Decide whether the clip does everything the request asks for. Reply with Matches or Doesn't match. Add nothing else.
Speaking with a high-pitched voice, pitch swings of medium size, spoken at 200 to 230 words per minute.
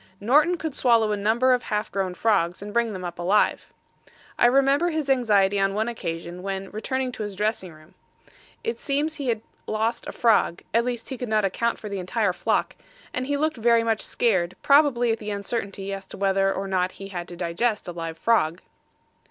Matches